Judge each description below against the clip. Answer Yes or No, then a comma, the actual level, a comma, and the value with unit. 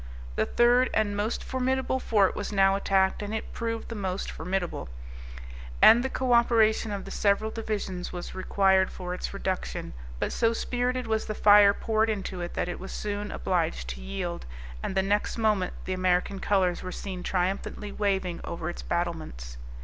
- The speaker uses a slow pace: No, average, 175 wpm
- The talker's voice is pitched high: Yes, high, 200 Hz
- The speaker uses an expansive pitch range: No, average, 3.3 semitones